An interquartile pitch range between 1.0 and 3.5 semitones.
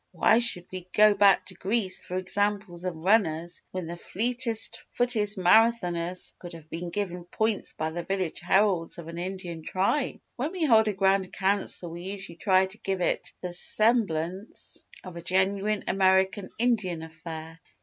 Yes: average, 3.2 semitones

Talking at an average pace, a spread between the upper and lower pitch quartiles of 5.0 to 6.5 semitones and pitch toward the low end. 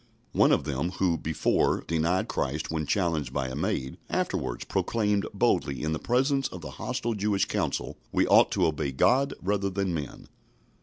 Yes: average, 170 wpm; wide, 5.4 semitones; very low, 85 Hz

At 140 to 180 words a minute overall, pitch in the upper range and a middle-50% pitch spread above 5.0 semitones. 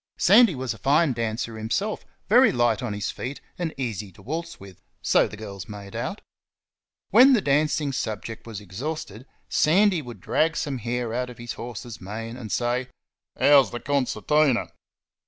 No: average, 165 wpm; low, 125 Hz; wide, 5.6 semitones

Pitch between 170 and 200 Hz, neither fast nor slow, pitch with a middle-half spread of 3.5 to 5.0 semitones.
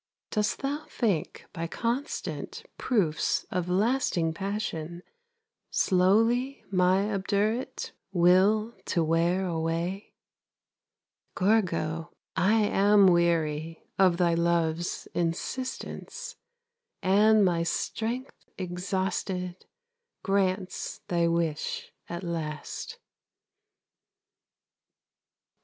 No: medium, 185 Hz; slow, 75 wpm; average, 3.8 semitones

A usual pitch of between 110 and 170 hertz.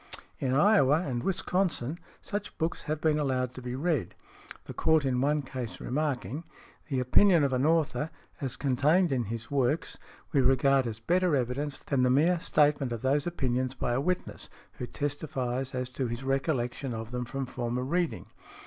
Yes: low, 135 Hz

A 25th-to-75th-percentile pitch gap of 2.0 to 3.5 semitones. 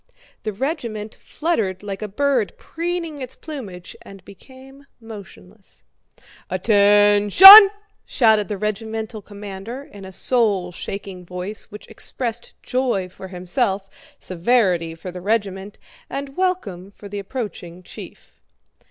No: average, 4.7 semitones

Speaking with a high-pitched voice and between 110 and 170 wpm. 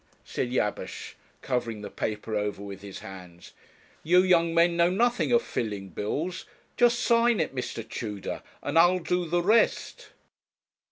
No: medium, 155 Hz; average, 150 wpm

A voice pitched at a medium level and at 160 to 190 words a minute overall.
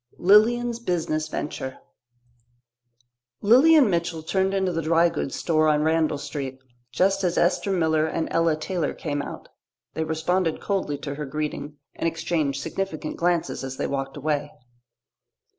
No: medium, 160 Hz; average, 140 wpm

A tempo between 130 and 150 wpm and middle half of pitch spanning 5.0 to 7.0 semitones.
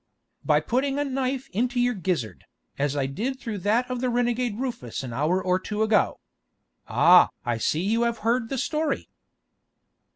No: average, 170 wpm; wide, 5.4 semitones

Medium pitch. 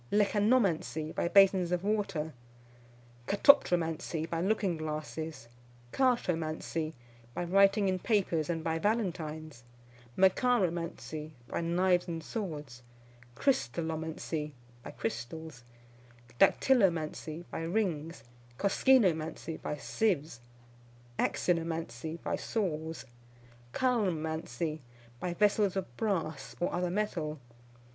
Yes: medium, 170 Hz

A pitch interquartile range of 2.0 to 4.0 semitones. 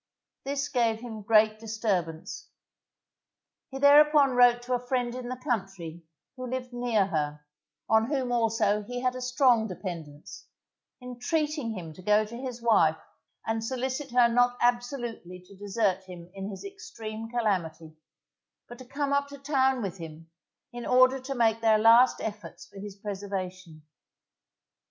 No: average, 4.4 semitones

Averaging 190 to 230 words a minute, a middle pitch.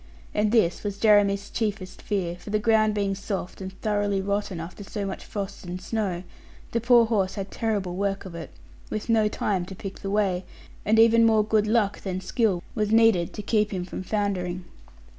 No: average, 195 wpm; high, 205 Hz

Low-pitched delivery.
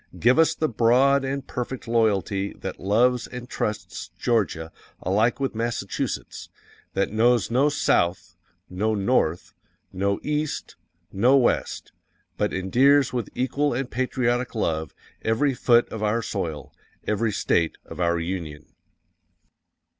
Yes: low, 115 Hz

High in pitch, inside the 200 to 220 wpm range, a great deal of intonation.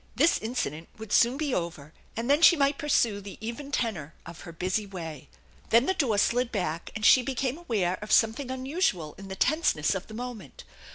Yes: high, 225 Hz; fast, 205 wpm; wide, 6.3 semitones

